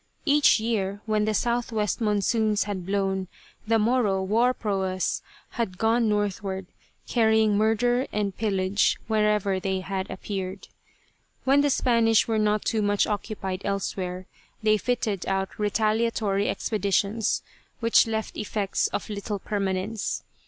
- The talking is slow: Yes, slow, 125 wpm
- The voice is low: No, high, 210 Hz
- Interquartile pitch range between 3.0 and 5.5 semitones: No, narrow, 2.4 semitones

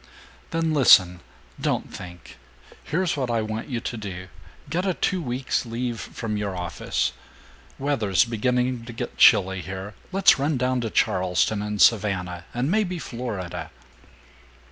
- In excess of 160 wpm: No, average, 145 wpm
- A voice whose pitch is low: Yes, low, 115 Hz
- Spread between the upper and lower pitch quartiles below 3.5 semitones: No, wide, 5.5 semitones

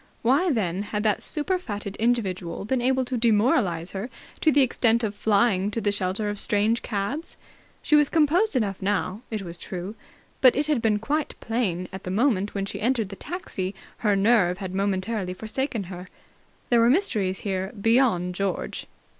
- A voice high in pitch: Yes, high, 210 Hz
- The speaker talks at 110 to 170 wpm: No, average, 180 wpm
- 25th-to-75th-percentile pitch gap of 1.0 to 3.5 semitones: No, average, 4.3 semitones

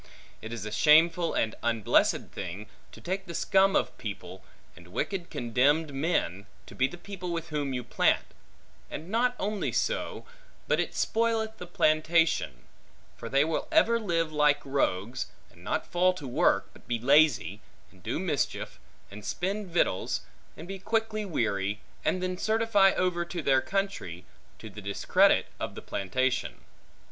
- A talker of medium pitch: Yes, medium, 160 Hz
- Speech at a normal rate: Yes, average, 160 wpm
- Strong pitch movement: Yes, wide, 8.1 semitones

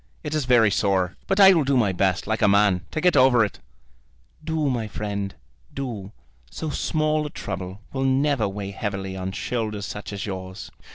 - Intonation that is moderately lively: No, wide, 5.9 semitones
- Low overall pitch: Yes, low, 105 Hz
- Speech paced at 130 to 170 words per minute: No, average, 185 wpm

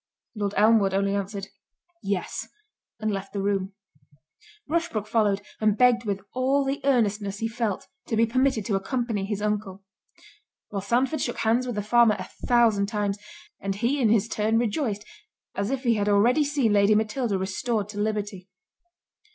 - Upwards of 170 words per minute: No, average, 165 wpm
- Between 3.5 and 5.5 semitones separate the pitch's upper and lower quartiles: No, average, 3.0 semitones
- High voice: Yes, high, 215 Hz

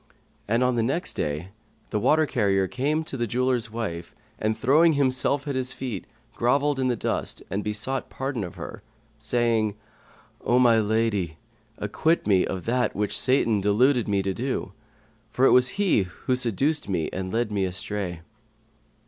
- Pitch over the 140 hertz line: No, low, 115 Hz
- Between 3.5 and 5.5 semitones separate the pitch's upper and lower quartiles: Yes, average, 4.4 semitones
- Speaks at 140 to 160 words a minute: No, average, 170 wpm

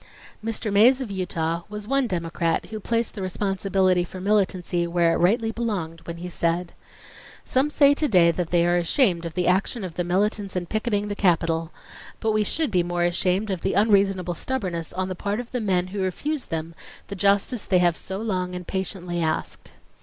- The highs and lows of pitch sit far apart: No, average, 3.4 semitones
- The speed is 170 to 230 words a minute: Yes, average, 200 wpm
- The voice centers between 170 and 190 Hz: Yes, medium, 185 Hz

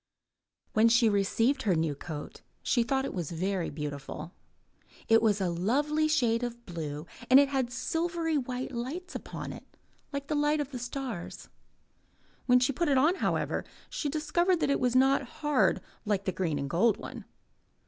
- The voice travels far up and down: Yes, wide, 6.7 semitones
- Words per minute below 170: No, average, 175 wpm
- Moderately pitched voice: No, high, 245 Hz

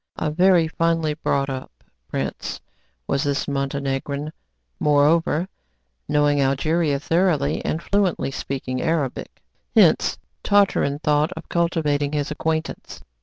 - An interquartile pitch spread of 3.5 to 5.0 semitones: No, average, 2.8 semitones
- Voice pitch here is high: No, medium, 150 Hz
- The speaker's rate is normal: No, slow, 110 wpm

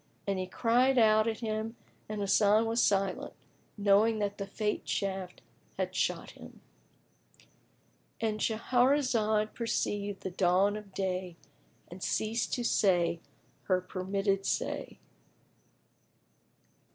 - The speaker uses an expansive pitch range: No, narrow, 2.5 semitones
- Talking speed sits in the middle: No, slow, 110 wpm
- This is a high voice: Yes, high, 205 Hz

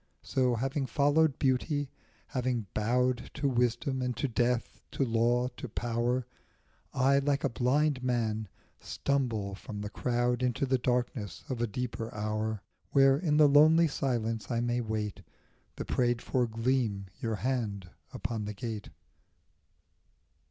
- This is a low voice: Yes, low, 125 Hz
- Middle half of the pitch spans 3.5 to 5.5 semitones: No, average, 2.9 semitones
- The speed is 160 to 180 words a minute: No, average, 140 wpm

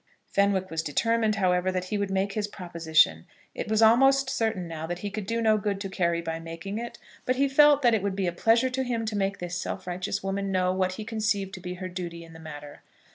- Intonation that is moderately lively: Yes, average, 3.7 semitones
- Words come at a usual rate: No, fast, 245 wpm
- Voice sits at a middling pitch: No, high, 195 Hz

